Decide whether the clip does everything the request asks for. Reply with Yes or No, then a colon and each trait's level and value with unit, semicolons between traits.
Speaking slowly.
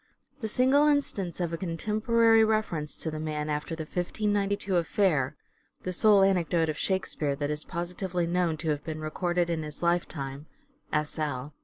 No: average, 170 wpm